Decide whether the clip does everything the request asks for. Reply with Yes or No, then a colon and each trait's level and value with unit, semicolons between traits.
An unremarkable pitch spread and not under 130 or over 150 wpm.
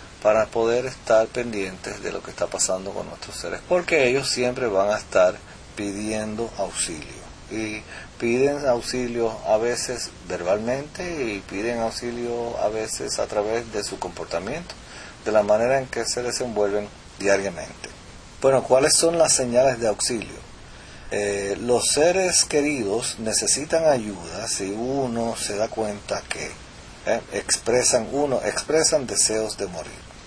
Yes: average, 3.4 semitones; average, 140 wpm